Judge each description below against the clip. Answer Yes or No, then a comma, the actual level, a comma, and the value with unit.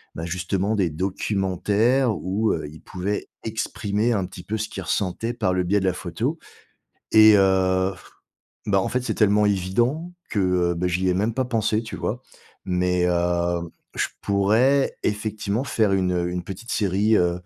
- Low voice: Yes, low, 100 Hz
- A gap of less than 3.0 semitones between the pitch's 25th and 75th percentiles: No, average, 3.3 semitones